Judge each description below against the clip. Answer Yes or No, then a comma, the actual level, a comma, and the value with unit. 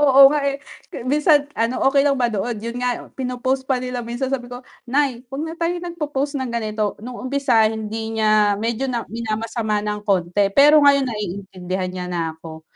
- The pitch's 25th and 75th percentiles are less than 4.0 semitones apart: No, average, 4.3 semitones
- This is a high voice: Yes, high, 240 Hz